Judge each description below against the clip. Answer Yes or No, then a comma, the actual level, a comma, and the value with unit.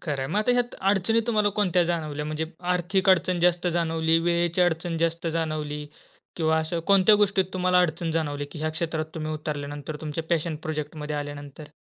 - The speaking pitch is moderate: Yes, medium, 165 Hz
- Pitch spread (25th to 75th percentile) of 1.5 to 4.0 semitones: Yes, average, 2.7 semitones